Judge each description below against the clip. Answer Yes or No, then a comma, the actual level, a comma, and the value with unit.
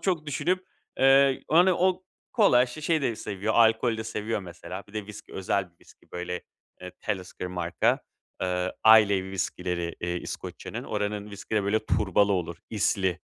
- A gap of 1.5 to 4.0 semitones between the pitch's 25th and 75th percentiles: No, average, 5.0 semitones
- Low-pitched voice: Yes, low, 105 Hz